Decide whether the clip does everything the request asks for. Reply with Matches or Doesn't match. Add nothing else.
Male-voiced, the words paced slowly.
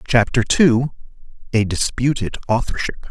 Matches